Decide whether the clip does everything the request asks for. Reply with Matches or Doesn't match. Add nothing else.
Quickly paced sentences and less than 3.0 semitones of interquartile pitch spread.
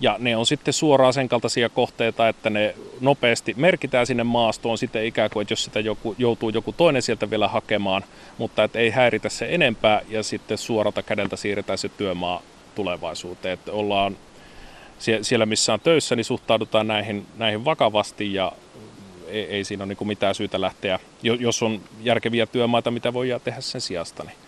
Matches